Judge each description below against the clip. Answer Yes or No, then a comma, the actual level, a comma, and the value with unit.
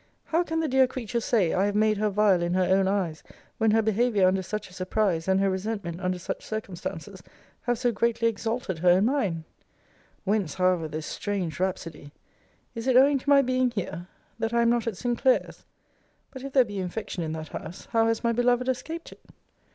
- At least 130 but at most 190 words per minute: No, fast, 205 wpm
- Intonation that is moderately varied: Yes, average, 4.6 semitones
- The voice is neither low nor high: No, high, 210 Hz